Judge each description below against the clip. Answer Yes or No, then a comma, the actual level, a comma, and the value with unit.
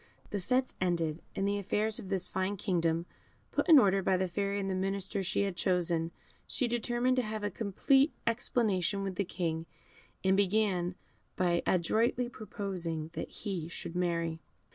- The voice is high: Yes, high, 195 Hz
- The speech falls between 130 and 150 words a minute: No, average, 165 wpm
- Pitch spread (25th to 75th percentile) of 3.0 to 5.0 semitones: Yes, average, 3.3 semitones